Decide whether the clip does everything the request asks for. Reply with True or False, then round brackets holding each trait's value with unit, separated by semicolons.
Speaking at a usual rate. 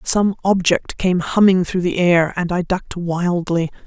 True (170 wpm)